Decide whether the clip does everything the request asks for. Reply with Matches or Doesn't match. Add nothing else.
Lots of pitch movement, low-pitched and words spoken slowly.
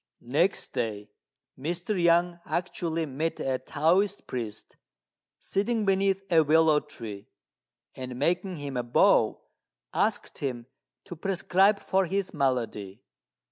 Doesn't match